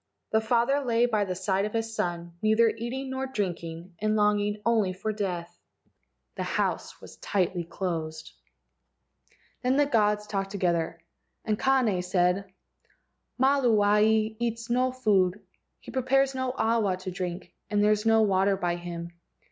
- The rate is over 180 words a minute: No, average, 150 wpm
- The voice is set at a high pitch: Yes, high, 210 Hz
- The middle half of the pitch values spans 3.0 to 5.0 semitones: Yes, average, 4.0 semitones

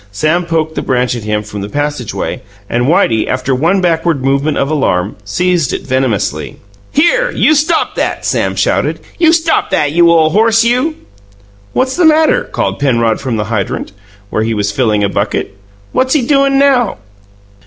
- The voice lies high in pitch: No, medium, 150 Hz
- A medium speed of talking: Yes, average, 175 wpm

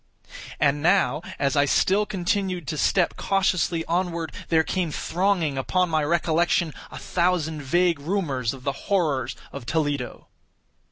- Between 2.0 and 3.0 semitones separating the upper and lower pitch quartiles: No, average, 3.9 semitones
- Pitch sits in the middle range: Yes, medium, 165 Hz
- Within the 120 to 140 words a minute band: Yes, slow, 135 wpm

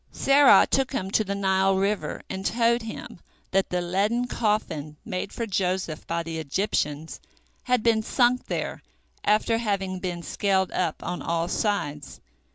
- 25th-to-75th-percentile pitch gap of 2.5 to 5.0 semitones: Yes, average, 3.9 semitones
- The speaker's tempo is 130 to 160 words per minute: Yes, average, 155 wpm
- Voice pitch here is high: Yes, high, 195 Hz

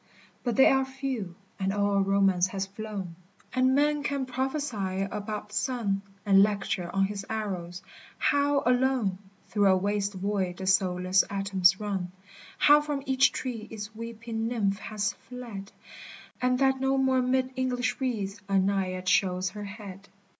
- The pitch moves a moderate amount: Yes, average, 4.7 semitones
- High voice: Yes, high, 210 Hz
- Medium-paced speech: Yes, average, 155 wpm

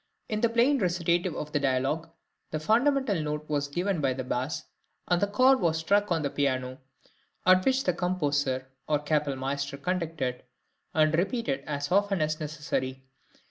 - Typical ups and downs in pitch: Yes, average, 4.6 semitones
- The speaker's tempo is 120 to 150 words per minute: No, average, 160 wpm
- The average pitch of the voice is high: No, medium, 155 Hz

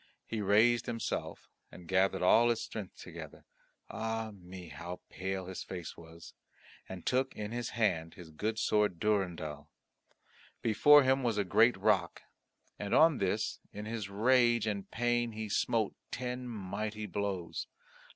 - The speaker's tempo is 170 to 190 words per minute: No, average, 145 wpm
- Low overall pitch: Yes, low, 105 Hz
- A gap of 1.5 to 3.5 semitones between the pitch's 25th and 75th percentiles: No, average, 3.9 semitones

